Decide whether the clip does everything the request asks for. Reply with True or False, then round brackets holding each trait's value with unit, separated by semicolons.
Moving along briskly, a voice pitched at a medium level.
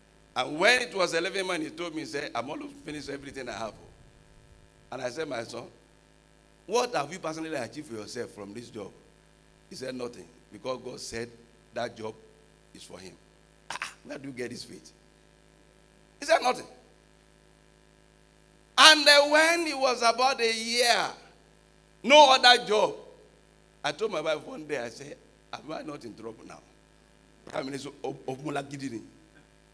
False (165 wpm; 160 Hz)